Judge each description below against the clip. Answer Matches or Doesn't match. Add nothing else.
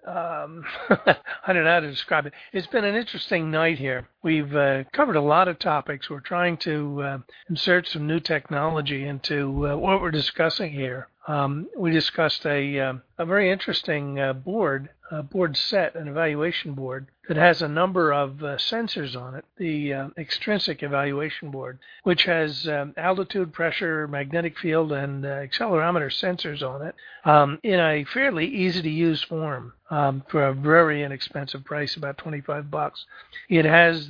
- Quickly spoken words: Doesn't match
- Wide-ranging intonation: Doesn't match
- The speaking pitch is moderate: Matches